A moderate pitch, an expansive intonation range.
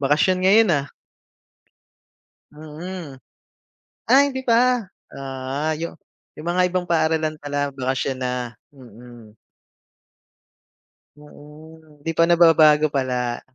No: medium, 155 Hz; average, 4.2 semitones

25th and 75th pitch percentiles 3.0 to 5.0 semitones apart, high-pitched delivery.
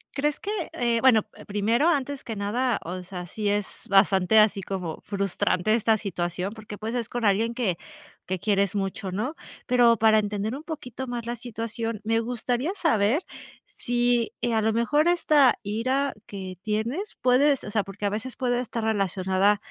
Yes: average, 3.4 semitones; high, 220 Hz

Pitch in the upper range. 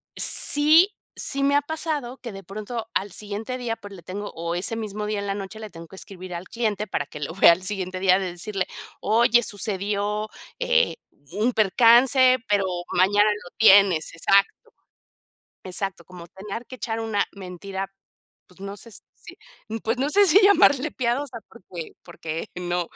Yes: high, 205 Hz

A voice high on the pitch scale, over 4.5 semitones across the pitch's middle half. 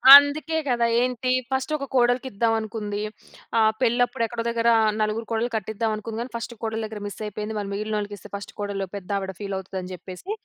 No: high, 220 Hz; average, 2.8 semitones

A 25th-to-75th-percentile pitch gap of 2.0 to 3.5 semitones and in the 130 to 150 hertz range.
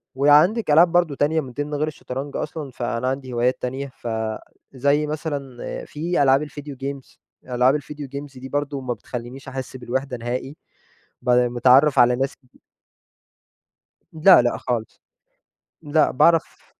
Yes: average, 2.8 semitones; low, 135 Hz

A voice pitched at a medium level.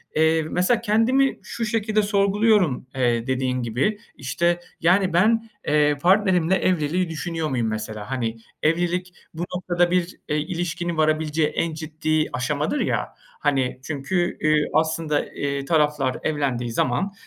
Yes: medium, 160 Hz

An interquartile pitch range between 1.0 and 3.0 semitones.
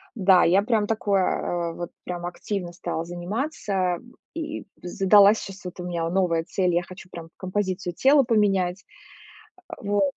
Yes: average, 2.7 semitones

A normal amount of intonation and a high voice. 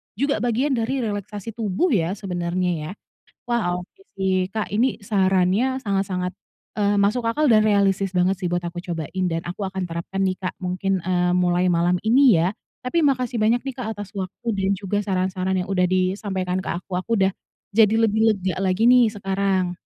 Yes: average, 3.1 semitones; high, 195 Hz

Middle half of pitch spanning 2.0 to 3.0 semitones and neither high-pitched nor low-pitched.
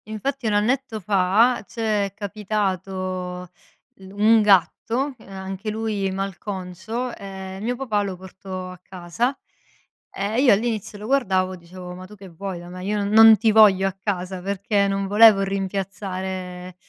No: narrow, 2.6 semitones; high, 195 Hz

